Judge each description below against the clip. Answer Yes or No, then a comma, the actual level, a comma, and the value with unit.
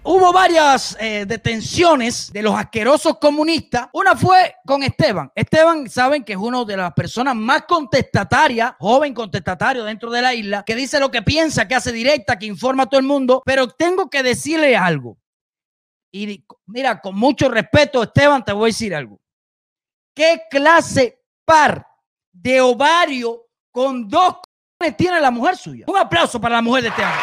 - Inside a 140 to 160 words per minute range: No, average, 170 wpm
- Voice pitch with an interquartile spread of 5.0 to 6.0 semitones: Yes, average, 5.3 semitones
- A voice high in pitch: Yes, very high, 260 Hz